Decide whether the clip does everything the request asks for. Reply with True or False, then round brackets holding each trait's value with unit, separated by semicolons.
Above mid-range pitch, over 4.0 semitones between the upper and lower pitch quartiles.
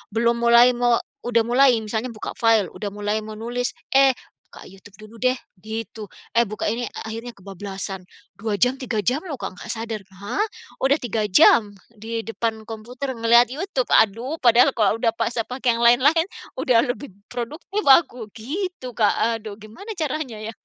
False (235 Hz; 2.7 semitones)